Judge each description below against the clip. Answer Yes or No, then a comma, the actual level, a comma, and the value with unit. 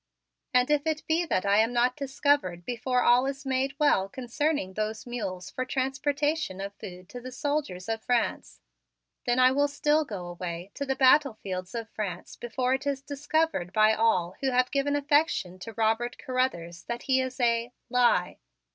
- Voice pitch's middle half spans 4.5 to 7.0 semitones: Yes, average, 5.1 semitones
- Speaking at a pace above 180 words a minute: No, average, 175 wpm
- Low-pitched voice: No, very high, 250 Hz